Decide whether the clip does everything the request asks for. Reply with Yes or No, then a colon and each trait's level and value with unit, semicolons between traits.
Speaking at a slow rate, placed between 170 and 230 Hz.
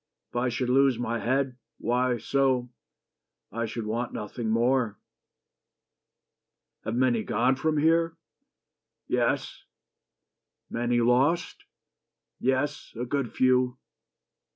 No: slow, 100 wpm; low, 125 Hz